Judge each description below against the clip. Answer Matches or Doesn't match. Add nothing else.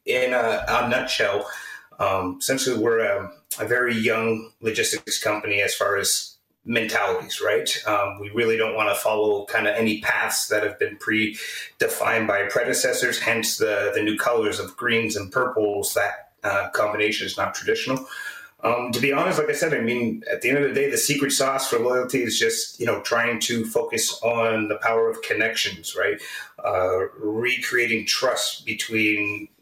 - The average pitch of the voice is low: Matches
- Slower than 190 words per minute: Matches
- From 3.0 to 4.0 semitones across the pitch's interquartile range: Matches